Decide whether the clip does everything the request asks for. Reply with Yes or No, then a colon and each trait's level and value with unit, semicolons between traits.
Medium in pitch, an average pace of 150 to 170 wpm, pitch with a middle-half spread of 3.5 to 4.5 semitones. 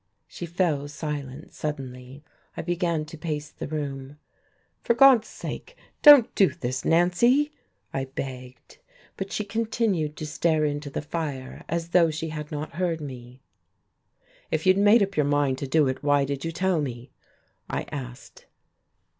Yes: medium, 155 Hz; average, 160 wpm; average, 4.1 semitones